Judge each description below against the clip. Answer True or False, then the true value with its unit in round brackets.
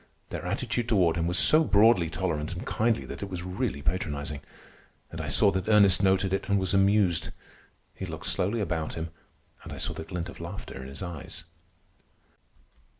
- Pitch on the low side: True (90 Hz)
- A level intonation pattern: False (3.3 semitones)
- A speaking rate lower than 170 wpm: False (185 wpm)